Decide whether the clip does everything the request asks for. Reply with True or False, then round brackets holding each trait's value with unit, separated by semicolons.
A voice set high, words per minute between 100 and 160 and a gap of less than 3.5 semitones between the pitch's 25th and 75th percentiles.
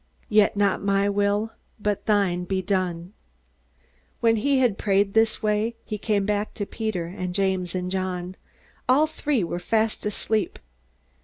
True (205 Hz; 150 wpm; 2.6 semitones)